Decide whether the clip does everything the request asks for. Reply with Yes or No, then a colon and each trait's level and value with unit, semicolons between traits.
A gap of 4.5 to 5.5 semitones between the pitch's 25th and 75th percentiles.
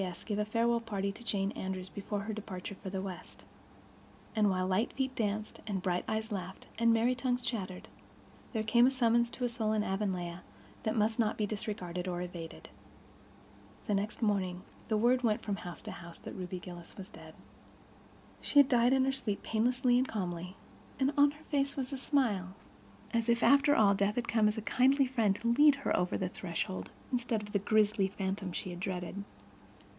No: average, 4.0 semitones